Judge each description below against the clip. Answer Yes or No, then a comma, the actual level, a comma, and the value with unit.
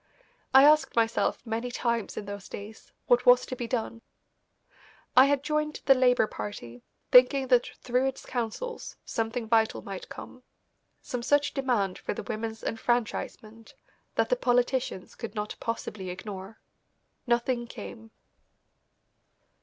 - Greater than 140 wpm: No, slow, 135 wpm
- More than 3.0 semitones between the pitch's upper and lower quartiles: No, narrow, 2.6 semitones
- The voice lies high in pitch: Yes, high, 235 Hz